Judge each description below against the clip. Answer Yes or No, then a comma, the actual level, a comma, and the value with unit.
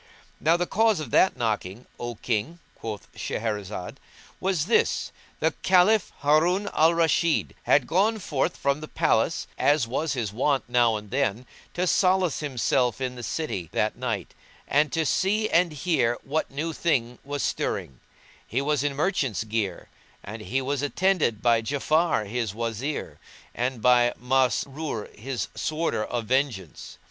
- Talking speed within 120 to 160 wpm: Yes, average, 150 wpm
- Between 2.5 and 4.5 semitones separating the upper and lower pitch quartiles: No, wide, 5.6 semitones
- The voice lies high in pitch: No, low, 135 Hz